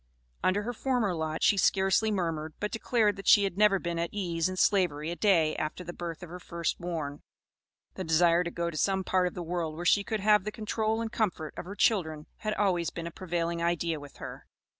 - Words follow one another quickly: Yes, fast, 225 wpm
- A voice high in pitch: No, medium, 180 Hz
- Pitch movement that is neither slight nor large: Yes, average, 3.5 semitones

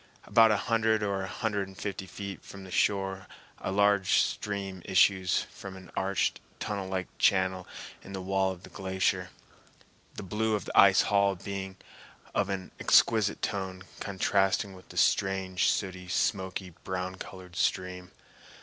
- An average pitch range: No, narrow, 1.2 semitones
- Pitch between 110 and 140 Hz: No, very low, 95 Hz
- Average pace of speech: Yes, average, 155 wpm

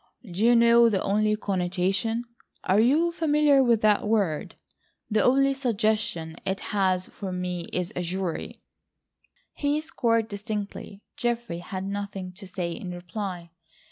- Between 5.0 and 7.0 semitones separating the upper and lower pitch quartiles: No, average, 4.2 semitones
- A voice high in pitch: Yes, high, 205 Hz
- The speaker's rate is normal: No, slow, 130 wpm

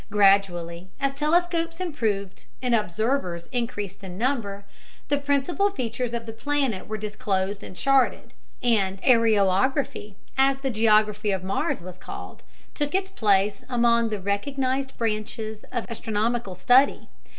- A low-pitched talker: No, high, 225 Hz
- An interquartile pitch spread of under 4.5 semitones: No, average, 5.0 semitones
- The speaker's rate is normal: No, slow, 130 wpm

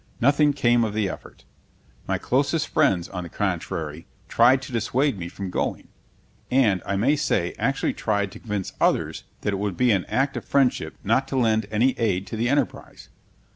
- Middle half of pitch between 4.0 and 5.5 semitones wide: Yes, average, 5.2 semitones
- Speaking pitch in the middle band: No, low, 110 Hz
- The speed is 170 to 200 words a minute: Yes, average, 185 wpm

